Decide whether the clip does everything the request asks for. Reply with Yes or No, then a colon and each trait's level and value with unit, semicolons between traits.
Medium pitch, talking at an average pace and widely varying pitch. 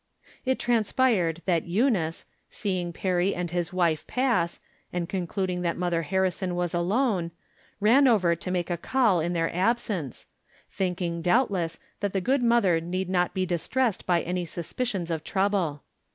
No: medium, 180 Hz; average, 155 wpm; average, 3.1 semitones